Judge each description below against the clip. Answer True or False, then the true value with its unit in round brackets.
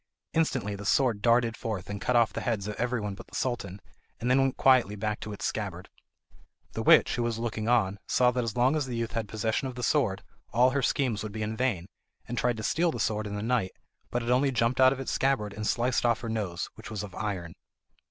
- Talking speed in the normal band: False (245 wpm)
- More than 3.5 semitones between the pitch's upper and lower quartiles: False (3.1 semitones)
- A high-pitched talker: False (115 Hz)